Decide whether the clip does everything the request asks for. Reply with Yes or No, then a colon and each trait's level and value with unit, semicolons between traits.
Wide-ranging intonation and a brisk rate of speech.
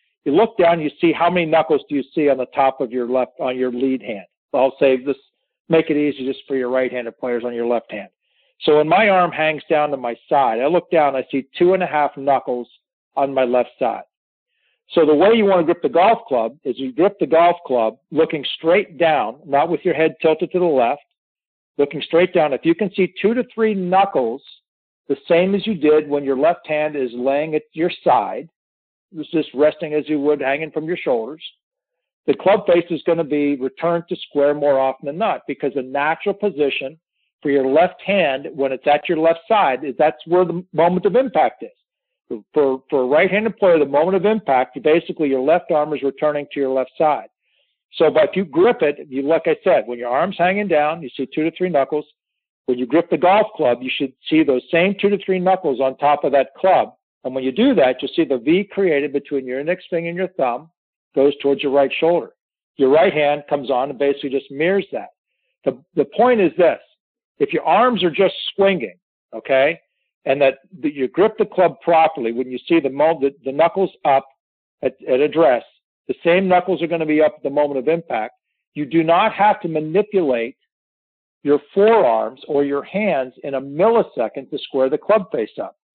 No: average, 4.6 semitones; fast, 220 wpm